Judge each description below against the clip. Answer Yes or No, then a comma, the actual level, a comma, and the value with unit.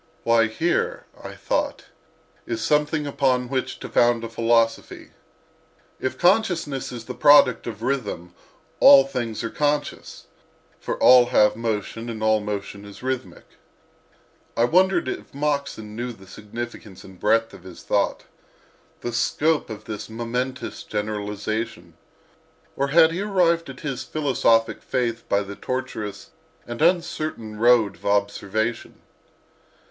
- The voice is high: No, low, 120 Hz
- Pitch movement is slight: No, average, 4.6 semitones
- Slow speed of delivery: Yes, slow, 130 wpm